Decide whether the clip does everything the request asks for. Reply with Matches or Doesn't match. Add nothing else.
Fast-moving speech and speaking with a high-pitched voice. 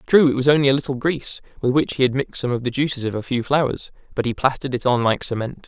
Doesn't match